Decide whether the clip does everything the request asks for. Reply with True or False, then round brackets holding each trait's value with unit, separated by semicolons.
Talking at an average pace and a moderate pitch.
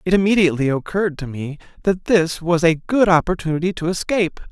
True (175 wpm; 175 Hz)